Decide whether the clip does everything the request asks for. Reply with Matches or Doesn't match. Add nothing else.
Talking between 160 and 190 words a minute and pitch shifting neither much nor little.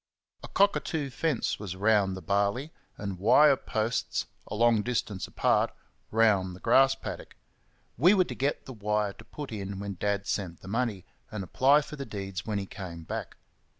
Matches